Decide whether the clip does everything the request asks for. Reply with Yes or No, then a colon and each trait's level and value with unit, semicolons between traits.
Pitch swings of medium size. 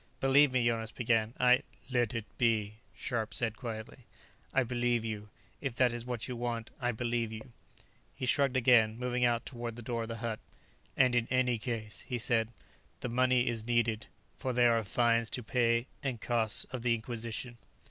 No: narrow, 1.6 semitones